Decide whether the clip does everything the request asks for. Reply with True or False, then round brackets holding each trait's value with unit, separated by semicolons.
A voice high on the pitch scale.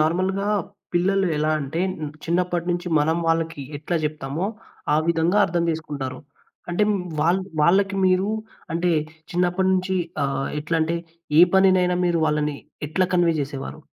False (170 Hz)